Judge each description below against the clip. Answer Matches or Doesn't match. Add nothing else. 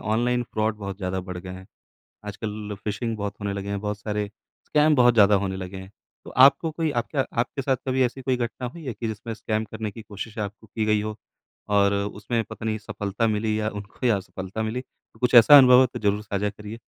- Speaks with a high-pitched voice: Doesn't match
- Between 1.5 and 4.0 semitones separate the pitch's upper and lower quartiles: Matches